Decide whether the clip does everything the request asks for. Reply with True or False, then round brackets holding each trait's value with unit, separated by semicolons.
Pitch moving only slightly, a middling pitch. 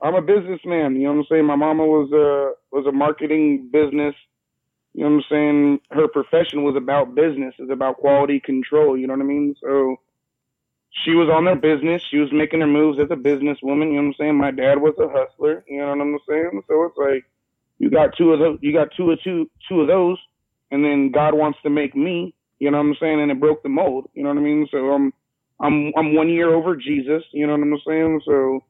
True (1.9 semitones; 150 Hz)